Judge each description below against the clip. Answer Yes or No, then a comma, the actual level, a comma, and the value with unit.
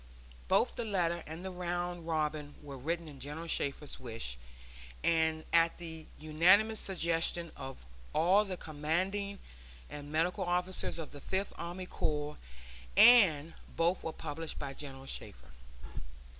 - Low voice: No, medium, 165 Hz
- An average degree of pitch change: Yes, average, 3.1 semitones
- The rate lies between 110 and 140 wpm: Yes, slow, 135 wpm